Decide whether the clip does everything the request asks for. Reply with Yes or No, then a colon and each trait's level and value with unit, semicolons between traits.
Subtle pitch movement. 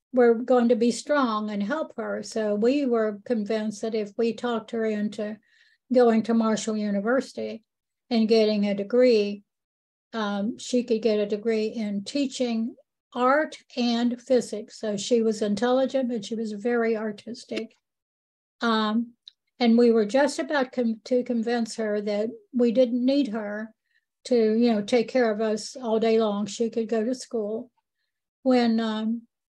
Yes: narrow, 2.3 semitones